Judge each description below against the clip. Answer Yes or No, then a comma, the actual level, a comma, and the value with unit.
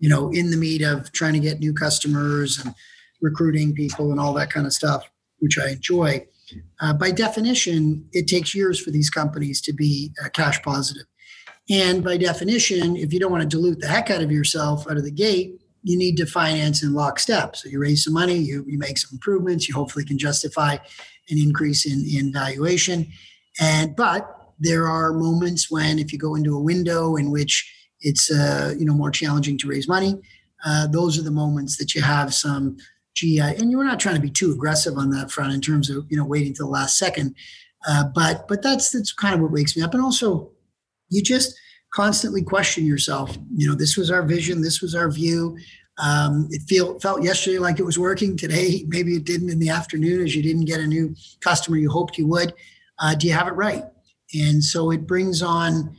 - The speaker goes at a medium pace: No, fast, 215 wpm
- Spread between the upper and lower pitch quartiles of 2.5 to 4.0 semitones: Yes, average, 3.2 semitones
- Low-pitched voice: No, medium, 160 Hz